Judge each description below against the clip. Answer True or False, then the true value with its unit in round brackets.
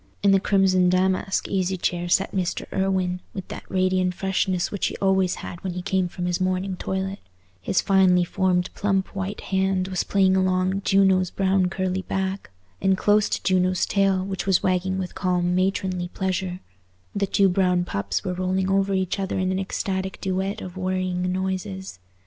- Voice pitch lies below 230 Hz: True (190 Hz)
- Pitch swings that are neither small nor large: False (0.9 semitones)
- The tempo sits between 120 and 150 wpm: False (175 wpm)